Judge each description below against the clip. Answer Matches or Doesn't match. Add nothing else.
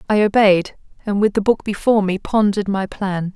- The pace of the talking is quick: Doesn't match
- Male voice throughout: Doesn't match